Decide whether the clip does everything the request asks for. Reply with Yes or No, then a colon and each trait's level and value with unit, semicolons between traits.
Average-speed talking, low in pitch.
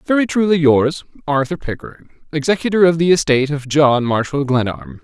No: average, 155 wpm; medium, 145 Hz